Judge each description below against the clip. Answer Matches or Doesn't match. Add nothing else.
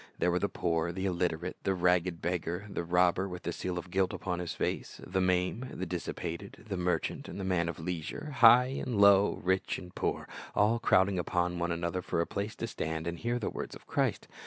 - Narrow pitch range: Matches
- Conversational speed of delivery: Doesn't match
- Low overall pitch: Matches